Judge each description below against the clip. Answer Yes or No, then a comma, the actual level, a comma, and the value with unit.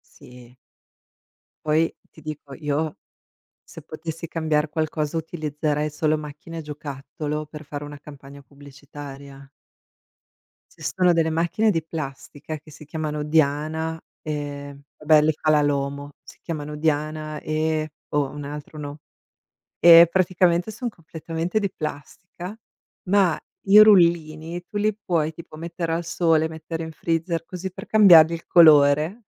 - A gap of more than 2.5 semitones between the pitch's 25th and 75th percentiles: No, narrow, 2.1 semitones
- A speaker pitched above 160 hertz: No, medium, 155 Hz